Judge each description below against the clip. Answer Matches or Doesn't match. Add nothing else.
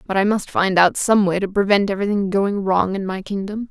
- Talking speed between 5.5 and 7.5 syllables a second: Matches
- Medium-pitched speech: Doesn't match